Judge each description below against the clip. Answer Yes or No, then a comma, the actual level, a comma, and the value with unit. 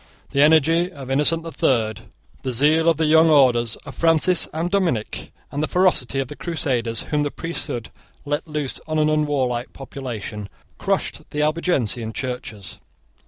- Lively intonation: No, average, 4.5 semitones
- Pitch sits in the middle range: Yes, medium, 145 Hz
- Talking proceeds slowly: No, average, 160 wpm